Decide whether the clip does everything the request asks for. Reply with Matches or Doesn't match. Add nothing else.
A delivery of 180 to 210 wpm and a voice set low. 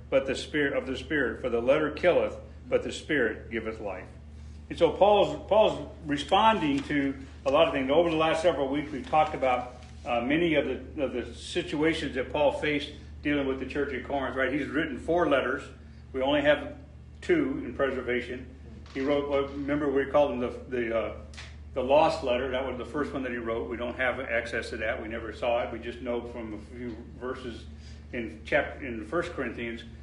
Matches